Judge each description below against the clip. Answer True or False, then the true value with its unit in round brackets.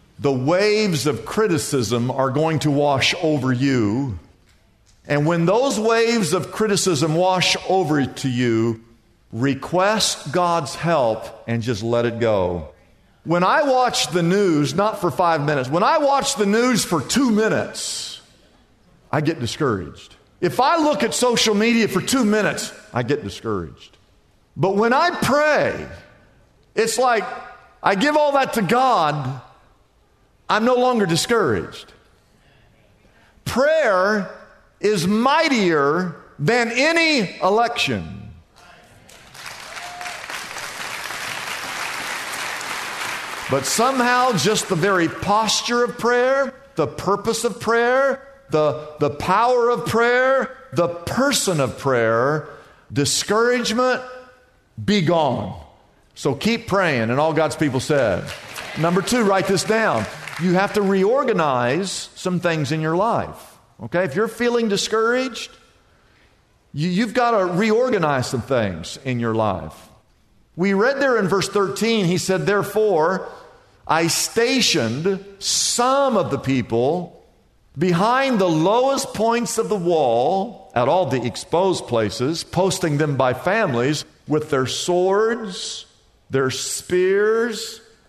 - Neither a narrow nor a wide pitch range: False (8.5 semitones)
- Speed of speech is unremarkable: False (120 wpm)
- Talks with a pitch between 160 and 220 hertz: True (185 Hz)